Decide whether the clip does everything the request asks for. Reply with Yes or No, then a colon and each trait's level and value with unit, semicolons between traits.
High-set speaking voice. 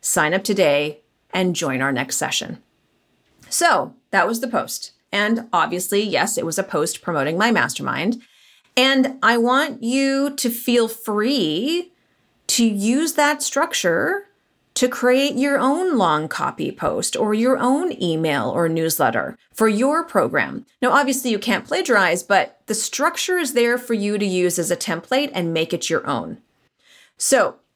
Yes: high, 240 Hz